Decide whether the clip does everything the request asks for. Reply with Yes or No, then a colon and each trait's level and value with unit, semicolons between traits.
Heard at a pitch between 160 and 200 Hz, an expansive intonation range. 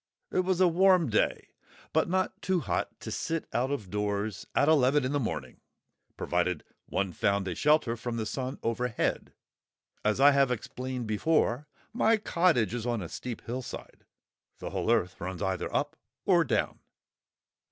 No: low, 125 Hz; wide, 6.3 semitones